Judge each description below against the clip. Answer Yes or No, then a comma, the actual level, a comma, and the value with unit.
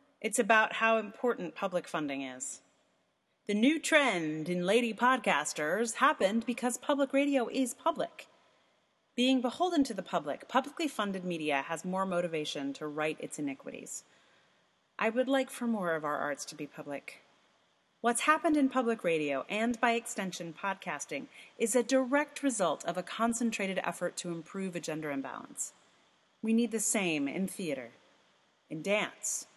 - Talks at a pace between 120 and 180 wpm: Yes, average, 150 wpm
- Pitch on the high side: Yes, high, 215 Hz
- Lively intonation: Yes, wide, 6.6 semitones